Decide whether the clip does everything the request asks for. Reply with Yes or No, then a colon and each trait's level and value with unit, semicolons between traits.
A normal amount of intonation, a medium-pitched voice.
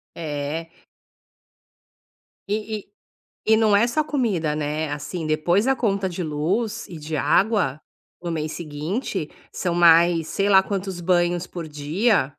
Yes: average, 4.6 semitones; medium, 175 Hz